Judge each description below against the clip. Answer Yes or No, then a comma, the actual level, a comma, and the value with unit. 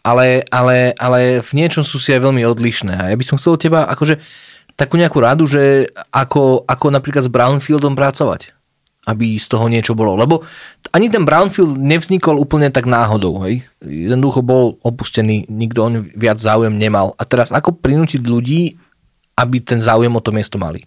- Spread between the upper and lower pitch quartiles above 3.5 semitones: Yes, average, 4.1 semitones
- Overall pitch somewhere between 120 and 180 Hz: Yes, low, 125 Hz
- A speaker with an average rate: No, fast, 180 wpm